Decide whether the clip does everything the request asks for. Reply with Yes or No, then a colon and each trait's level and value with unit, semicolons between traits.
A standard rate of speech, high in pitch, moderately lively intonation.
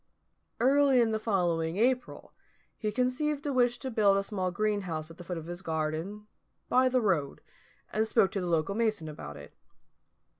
No: average, 180 wpm; high, 205 Hz; wide, 6.4 semitones